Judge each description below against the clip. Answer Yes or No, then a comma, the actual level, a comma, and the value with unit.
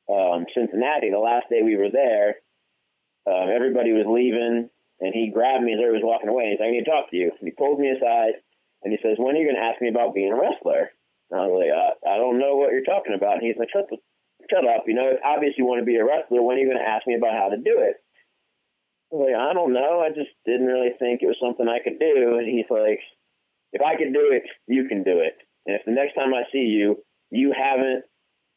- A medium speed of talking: No, fast, 270 wpm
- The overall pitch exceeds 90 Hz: Yes, low, 125 Hz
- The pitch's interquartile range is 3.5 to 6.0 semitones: Yes, average, 3.9 semitones